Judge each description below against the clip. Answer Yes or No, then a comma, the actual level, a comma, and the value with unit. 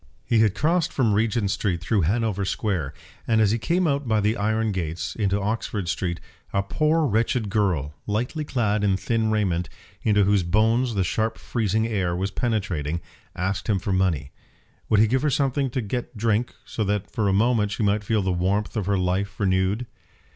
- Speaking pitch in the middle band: No, low, 105 Hz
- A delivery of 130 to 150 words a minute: No, average, 190 wpm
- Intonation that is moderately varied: Yes, average, 3.0 semitones